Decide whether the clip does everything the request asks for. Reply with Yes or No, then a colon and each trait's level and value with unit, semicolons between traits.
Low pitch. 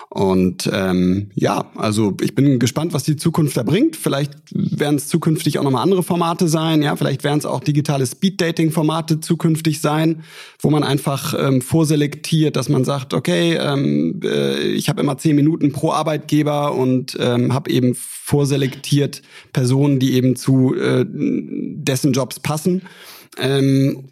No: medium, 145 Hz